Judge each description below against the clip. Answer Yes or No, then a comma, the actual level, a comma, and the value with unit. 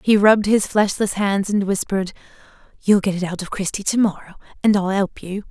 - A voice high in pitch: Yes, high, 195 Hz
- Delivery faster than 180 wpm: Yes, fast, 205 wpm